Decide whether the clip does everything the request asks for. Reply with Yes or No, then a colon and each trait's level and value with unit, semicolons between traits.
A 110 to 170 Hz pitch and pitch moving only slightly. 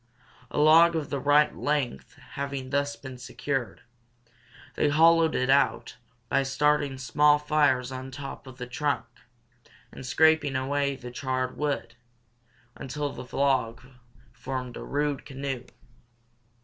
Yes: medium, 140 Hz; narrow, 2.3 semitones